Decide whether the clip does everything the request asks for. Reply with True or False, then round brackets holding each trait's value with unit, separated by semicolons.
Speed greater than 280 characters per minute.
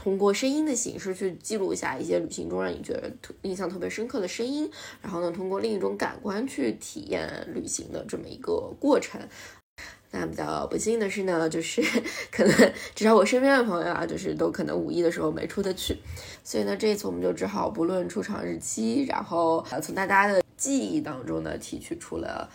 True (315 characters per minute)